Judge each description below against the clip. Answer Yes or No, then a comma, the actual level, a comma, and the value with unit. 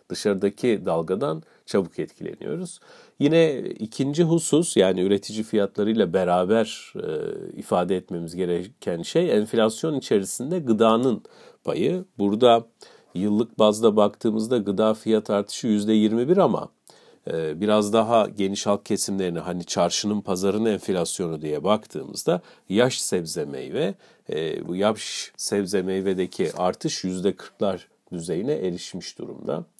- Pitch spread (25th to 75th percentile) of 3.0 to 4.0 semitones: Yes, average, 3.5 semitones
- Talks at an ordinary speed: Yes, average, 110 wpm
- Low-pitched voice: Yes, low, 105 Hz